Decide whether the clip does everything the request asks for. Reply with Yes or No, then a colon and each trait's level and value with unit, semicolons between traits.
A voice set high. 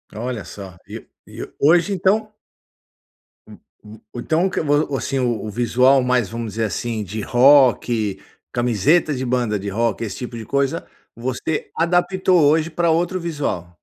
No: low, 125 Hz